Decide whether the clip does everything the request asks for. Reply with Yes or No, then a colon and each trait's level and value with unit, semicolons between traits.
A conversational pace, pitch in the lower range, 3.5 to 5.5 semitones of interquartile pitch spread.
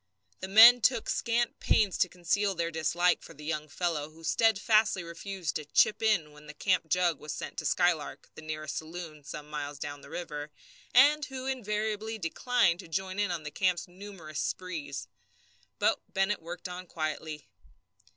No: average, 170 wpm; medium, 175 Hz; average, 5.0 semitones